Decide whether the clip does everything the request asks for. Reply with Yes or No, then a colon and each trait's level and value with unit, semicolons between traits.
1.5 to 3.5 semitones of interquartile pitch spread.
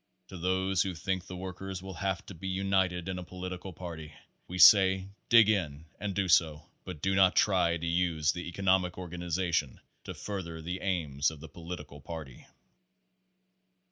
Yes: narrow, 2.5 semitones